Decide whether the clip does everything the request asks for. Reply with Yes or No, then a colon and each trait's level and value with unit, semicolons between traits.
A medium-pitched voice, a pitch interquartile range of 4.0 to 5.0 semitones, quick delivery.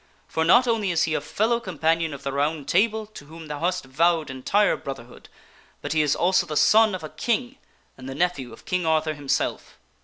Yes: medium, 160 Hz; average, 4.6 semitones; fast, 210 wpm